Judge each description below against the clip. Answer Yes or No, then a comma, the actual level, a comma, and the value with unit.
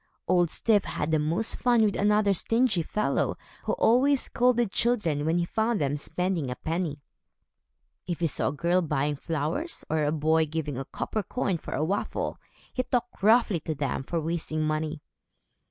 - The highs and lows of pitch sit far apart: Yes, wide, 5.8 semitones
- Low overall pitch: No, medium, 170 Hz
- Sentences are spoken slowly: No, average, 175 wpm